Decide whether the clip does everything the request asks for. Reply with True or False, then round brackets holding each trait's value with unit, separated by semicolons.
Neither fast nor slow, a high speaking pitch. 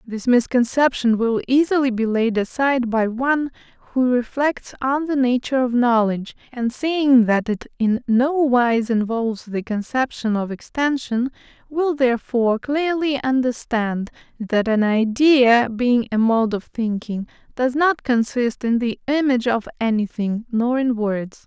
True (145 wpm; 245 Hz)